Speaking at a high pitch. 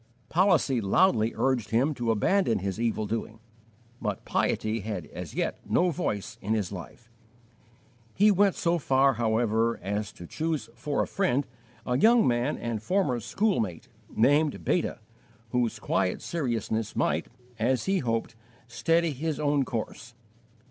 No: low, 120 Hz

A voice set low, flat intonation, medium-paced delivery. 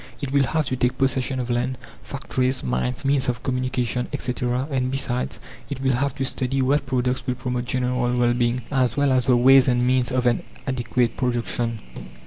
Yes: low, 125 Hz; narrow, 1.5 semitones; average, 190 wpm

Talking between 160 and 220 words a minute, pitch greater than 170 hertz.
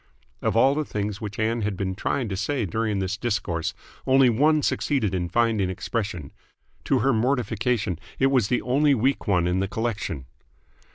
No: average, 175 wpm; low, 110 Hz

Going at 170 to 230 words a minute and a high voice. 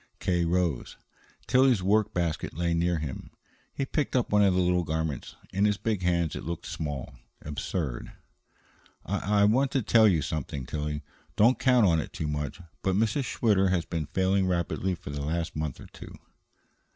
No: average, 180 wpm; very low, 90 Hz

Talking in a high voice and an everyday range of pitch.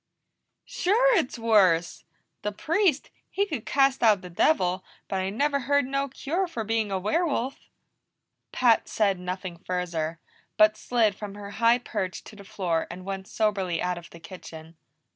No: high, 210 Hz; wide, 6.6 semitones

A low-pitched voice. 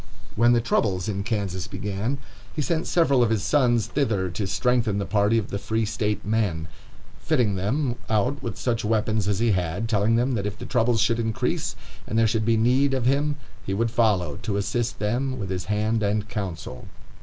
Yes: low, 110 Hz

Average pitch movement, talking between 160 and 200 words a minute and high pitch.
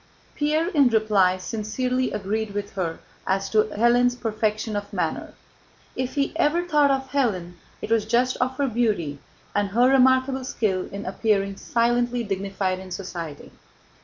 No: average, 4.5 semitones; average, 150 wpm; high, 220 Hz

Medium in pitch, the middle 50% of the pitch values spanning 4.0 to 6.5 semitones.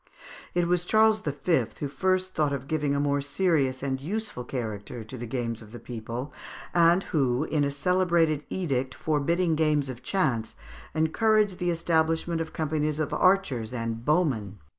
Yes: medium, 150 Hz; average, 5.1 semitones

